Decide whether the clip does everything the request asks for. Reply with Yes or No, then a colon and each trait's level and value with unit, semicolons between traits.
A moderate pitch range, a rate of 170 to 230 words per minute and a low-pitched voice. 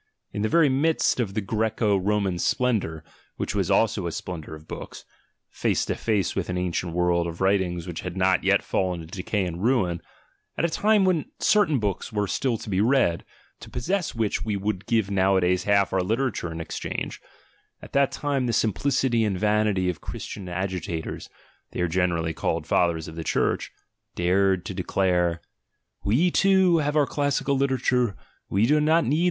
No: wide, 5.9 semitones; average, 180 wpm; low, 100 Hz